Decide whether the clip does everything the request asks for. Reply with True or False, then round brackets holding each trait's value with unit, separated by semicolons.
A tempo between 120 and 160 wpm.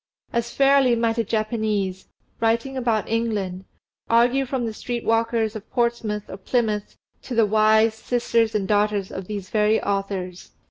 True (150 wpm)